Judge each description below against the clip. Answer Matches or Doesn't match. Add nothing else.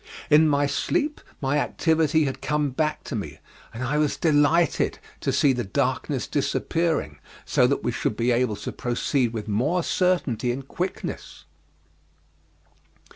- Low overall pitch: Doesn't match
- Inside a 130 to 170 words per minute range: Matches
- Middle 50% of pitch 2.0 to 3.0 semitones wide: Doesn't match